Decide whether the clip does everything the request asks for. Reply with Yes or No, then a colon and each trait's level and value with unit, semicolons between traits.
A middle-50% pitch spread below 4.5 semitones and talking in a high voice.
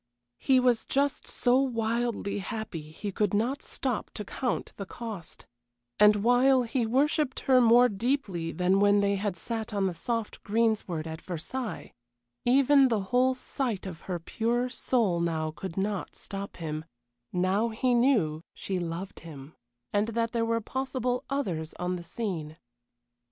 No: average, 5.3 semitones; high, 220 Hz